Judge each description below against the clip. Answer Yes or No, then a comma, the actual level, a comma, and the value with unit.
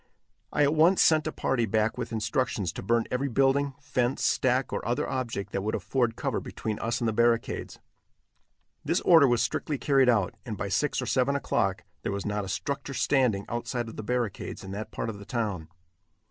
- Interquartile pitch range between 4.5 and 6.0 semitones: No, average, 3.9 semitones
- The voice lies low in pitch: Yes, low, 120 Hz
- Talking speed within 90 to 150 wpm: No, average, 200 wpm